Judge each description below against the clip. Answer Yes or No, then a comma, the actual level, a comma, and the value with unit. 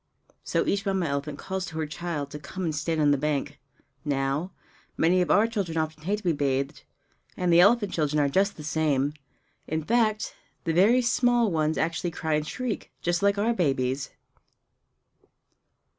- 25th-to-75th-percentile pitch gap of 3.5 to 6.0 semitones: Yes, average, 4.7 semitones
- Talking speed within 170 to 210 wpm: Yes, average, 175 wpm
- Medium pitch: Yes, medium, 160 Hz